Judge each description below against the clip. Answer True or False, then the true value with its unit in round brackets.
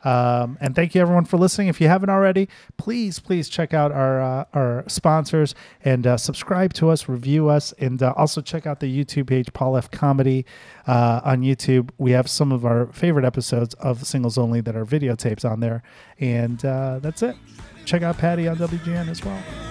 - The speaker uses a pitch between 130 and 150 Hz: True (140 Hz)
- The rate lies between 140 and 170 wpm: False (200 wpm)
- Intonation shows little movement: False (4.6 semitones)